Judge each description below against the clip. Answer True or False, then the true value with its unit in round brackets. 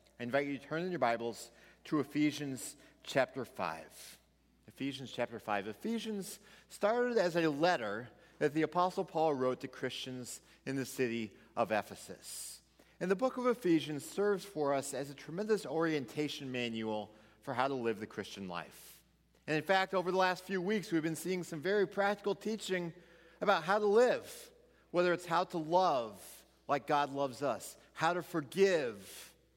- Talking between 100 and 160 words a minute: False (170 wpm)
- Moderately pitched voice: True (160 Hz)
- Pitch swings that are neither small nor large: False (6.1 semitones)